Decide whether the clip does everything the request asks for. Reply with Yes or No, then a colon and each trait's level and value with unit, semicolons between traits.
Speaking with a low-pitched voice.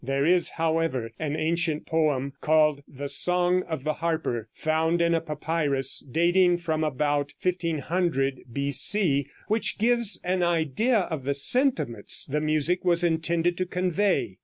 No: medium, 160 Hz